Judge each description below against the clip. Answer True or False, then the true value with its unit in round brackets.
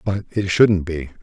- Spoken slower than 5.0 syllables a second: True (3.9 syllables/s)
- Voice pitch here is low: True (90 Hz)